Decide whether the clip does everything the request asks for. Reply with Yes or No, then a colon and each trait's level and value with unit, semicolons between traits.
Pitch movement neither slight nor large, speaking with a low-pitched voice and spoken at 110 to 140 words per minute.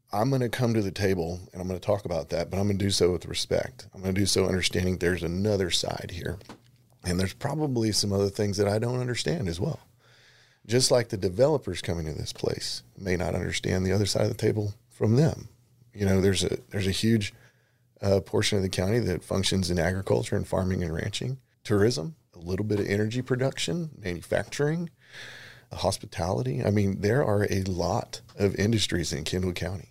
No: average, 4.1 semitones; low, 100 Hz; fast, 205 wpm